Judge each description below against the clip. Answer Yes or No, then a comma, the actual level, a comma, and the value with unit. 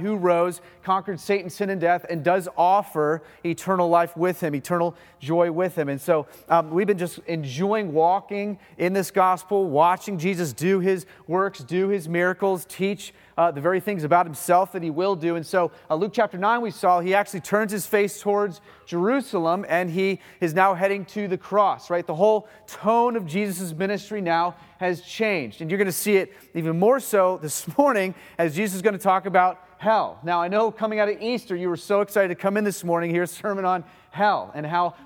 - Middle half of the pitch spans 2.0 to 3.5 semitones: Yes, average, 2.7 semitones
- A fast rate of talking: Yes, fast, 210 wpm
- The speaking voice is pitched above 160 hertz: Yes, medium, 185 Hz